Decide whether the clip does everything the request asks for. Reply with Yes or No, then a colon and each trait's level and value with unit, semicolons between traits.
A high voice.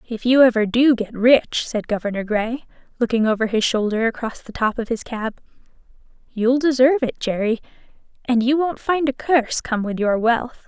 Yes: high, 240 Hz